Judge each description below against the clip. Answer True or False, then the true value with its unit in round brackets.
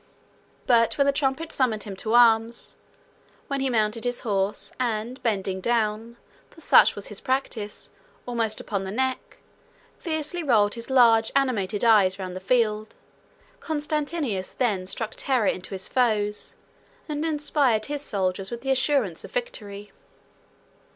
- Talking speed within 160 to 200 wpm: False (145 wpm)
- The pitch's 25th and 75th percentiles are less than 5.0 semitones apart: True (4.4 semitones)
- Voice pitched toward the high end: True (230 Hz)